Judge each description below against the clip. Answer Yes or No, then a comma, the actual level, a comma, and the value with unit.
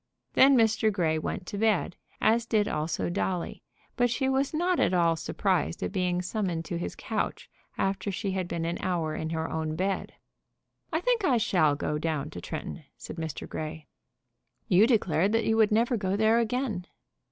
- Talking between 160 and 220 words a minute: Yes, average, 185 wpm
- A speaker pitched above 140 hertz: Yes, high, 190 Hz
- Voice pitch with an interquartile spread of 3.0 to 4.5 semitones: No, average, 5.2 semitones